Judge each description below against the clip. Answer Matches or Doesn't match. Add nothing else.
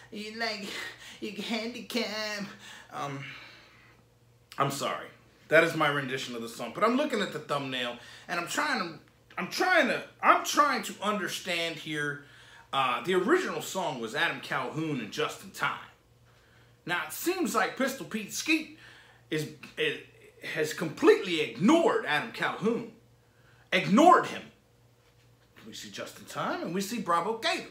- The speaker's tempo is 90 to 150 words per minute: Matches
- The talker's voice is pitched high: Matches